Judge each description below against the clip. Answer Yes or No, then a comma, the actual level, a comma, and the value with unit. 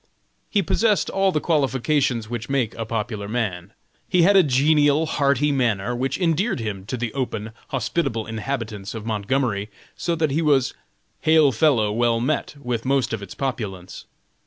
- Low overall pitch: Yes, low, 125 Hz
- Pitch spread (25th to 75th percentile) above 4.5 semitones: Yes, average, 5.1 semitones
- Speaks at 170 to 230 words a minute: No, average, 160 wpm